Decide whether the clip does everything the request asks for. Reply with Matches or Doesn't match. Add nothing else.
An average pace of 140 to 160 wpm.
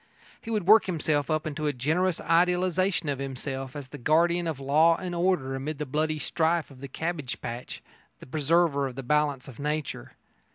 Doesn't match